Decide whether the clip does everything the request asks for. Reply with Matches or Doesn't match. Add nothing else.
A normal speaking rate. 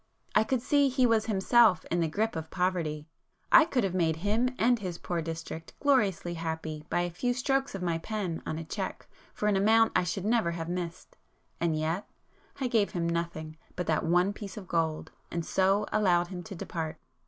Matches